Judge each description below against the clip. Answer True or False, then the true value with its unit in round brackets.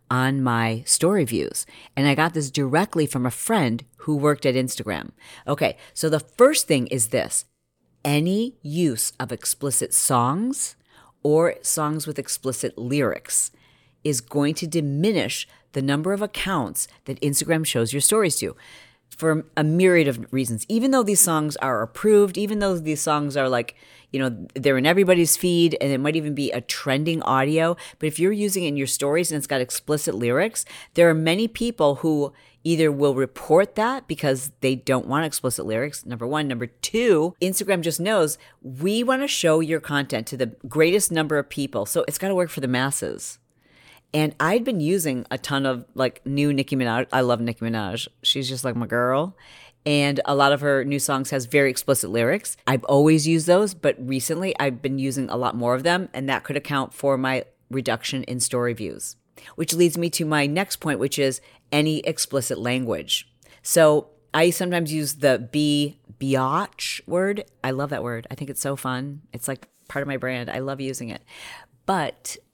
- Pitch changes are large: False (3.8 semitones)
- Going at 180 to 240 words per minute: True (190 wpm)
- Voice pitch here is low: False (145 Hz)